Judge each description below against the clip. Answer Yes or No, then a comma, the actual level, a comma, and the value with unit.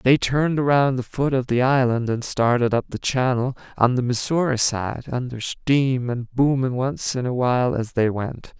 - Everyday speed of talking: Yes, average, 195 wpm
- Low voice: Yes, low, 125 Hz